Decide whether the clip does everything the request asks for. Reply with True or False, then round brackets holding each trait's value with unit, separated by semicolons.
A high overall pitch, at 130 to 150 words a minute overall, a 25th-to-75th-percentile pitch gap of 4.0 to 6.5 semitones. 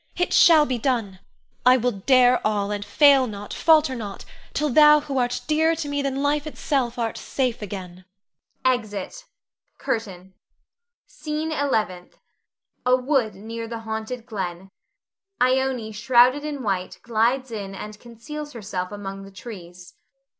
True (240 Hz; 140 wpm; 5.1 semitones)